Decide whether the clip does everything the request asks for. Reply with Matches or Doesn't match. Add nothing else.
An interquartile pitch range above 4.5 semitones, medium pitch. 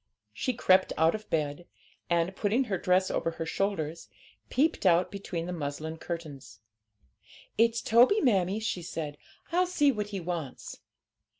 Matches